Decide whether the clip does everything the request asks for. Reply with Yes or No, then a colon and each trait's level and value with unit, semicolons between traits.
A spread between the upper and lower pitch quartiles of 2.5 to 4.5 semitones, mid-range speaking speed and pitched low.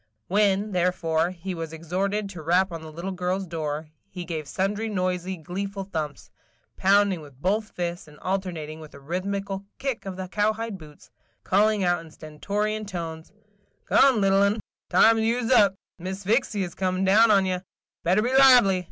No: average, 3.3 semitones; average, 175 wpm; high, 190 Hz